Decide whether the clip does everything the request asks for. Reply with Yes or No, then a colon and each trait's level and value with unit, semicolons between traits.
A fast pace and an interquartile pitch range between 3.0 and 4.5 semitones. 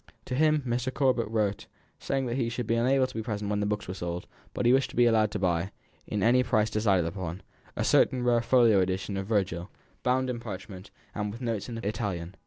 Yes: fast, 235 wpm; average, 3.9 semitones